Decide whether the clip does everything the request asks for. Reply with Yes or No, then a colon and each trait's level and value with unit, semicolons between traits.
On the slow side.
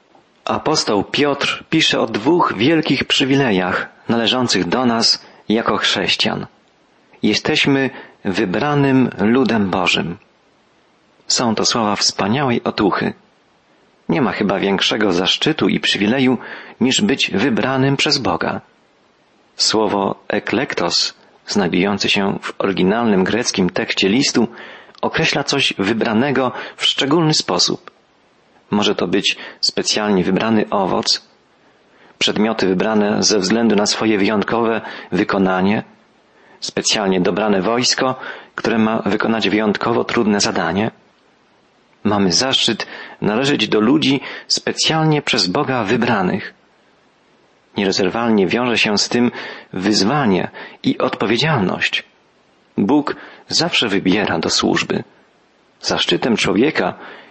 Yes: slow, 100 wpm